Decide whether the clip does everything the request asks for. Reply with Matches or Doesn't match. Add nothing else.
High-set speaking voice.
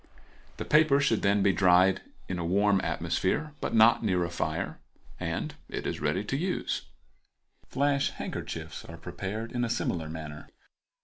Doesn't match